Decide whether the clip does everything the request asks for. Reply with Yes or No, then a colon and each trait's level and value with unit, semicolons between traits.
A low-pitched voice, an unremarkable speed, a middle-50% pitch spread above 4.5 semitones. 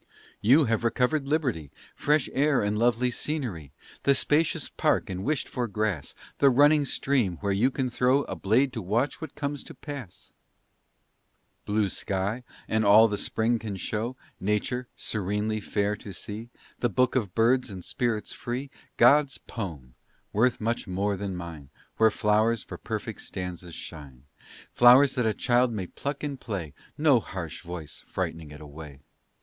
Yes: low, 110 Hz; average, 160 wpm; average, 5.0 semitones